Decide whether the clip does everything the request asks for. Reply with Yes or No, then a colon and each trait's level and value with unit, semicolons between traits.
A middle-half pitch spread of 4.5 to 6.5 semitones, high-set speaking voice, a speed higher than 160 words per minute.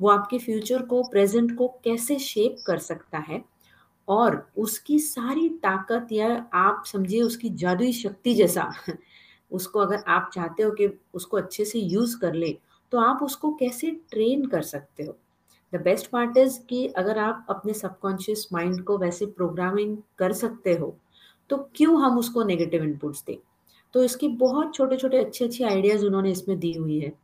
Yes: average, 5.0 semitones; high, 215 Hz; average, 170 wpm